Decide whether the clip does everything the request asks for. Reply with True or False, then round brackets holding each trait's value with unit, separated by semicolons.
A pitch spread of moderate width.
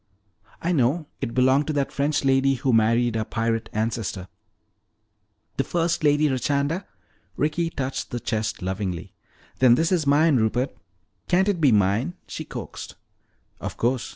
True (5.0 semitones)